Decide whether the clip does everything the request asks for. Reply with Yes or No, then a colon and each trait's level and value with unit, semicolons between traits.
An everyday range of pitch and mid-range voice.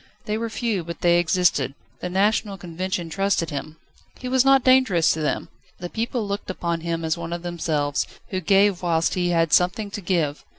Yes: average, 3.5 semitones; medium, 180 Hz